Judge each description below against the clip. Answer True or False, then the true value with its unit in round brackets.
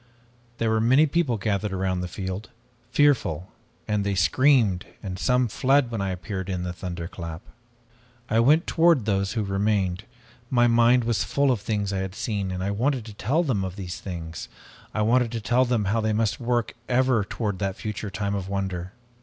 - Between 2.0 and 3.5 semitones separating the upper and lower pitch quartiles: False (4.1 semitones)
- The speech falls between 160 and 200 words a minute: True (190 wpm)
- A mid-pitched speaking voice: False (105 Hz)